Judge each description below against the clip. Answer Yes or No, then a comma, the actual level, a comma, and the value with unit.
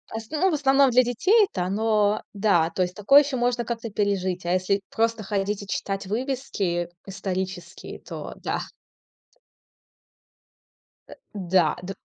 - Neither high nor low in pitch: No, high, 205 Hz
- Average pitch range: Yes, average, 4.3 semitones